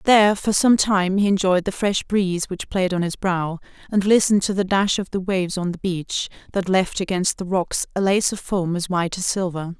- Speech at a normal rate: No, fast, 235 wpm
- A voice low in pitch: No, high, 190 Hz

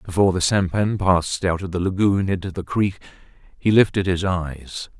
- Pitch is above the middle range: No, very low, 95 Hz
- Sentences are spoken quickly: No, average, 180 wpm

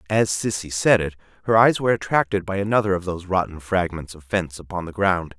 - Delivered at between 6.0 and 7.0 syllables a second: Yes, 6.1 syllables/s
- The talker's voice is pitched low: Yes, very low, 95 Hz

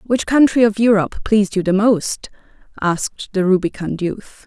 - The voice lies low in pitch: No, high, 205 Hz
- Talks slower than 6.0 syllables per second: Yes, 5.0 syllables/s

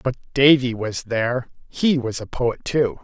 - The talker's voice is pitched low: Yes, low, 125 Hz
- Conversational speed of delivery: Yes, average, 180 wpm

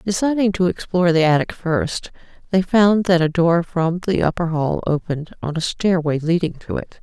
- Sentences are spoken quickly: No, average, 190 wpm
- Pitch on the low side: No, medium, 170 Hz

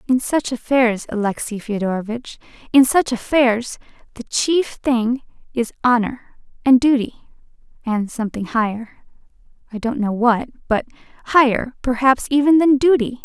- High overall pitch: Yes, high, 245 Hz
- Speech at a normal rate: No, slow, 120 wpm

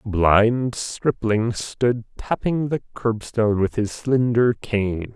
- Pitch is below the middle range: Yes, low, 115 Hz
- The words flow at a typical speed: No, slow, 130 wpm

